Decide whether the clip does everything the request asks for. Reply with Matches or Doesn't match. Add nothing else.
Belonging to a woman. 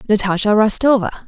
Matches